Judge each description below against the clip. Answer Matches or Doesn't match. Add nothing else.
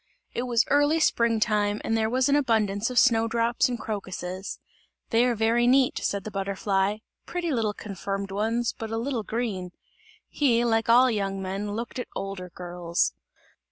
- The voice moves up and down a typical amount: Matches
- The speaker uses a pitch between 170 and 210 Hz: Doesn't match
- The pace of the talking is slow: Doesn't match